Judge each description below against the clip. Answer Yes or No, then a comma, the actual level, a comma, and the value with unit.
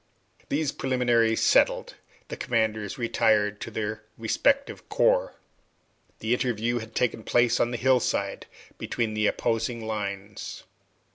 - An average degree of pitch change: No, narrow, 2.2 semitones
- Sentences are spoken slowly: Yes, slow, 120 wpm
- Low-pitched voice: Yes, low, 115 Hz